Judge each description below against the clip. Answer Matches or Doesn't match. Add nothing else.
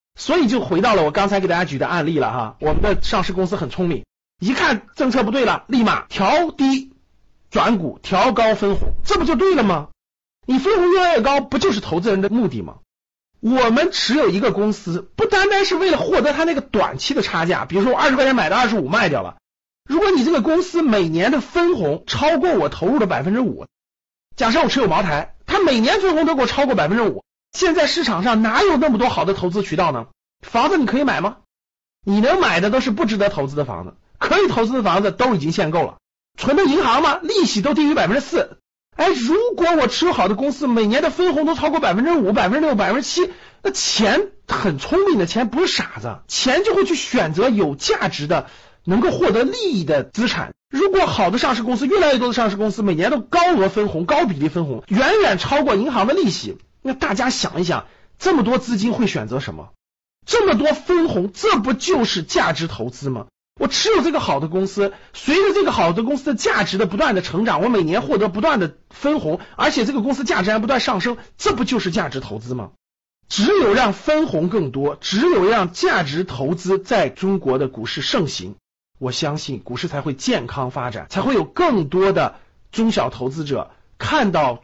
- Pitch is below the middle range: Doesn't match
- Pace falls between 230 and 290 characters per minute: Doesn't match